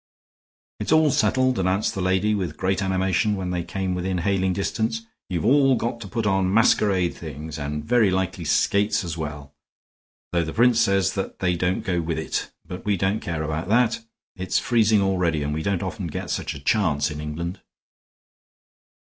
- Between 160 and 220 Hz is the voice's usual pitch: No, very low, 95 Hz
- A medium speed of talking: Yes, average, 180 wpm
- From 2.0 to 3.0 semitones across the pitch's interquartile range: No, average, 3.9 semitones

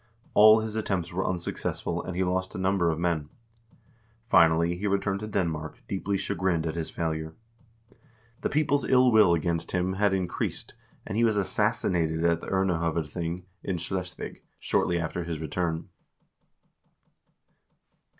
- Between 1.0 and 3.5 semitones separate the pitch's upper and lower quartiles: Yes, average, 2.8 semitones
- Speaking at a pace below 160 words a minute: Yes, average, 145 wpm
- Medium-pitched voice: No, very low, 90 Hz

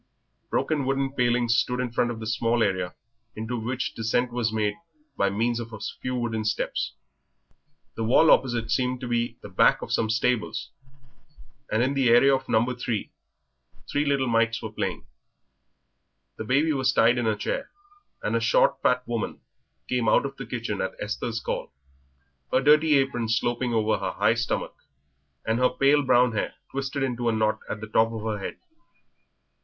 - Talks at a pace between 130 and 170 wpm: No, average, 180 wpm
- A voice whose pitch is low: Yes, low, 120 Hz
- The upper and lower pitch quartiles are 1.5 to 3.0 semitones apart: Yes, narrow, 2.5 semitones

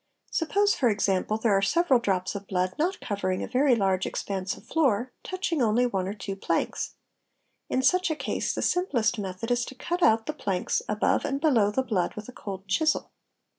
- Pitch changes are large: Yes, wide, 6.3 semitones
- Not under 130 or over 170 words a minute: No, average, 200 wpm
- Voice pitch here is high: Yes, high, 225 Hz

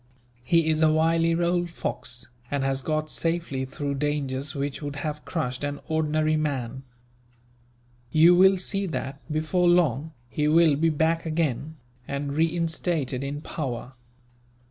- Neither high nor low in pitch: Yes, medium, 155 Hz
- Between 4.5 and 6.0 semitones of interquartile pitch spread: No, average, 2.9 semitones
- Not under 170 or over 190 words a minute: No, average, 140 wpm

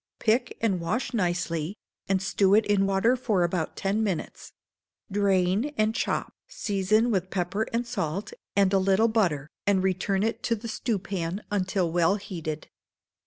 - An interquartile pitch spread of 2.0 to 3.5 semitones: Yes, average, 3.0 semitones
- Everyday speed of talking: Yes, average, 155 wpm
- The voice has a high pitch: Yes, high, 195 Hz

